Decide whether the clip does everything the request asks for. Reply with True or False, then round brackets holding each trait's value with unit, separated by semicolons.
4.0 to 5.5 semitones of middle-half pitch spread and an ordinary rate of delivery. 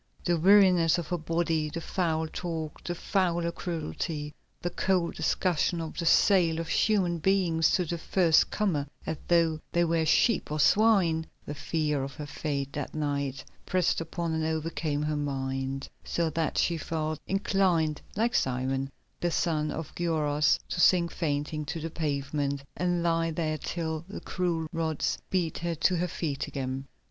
False (2.5 semitones; 165 wpm)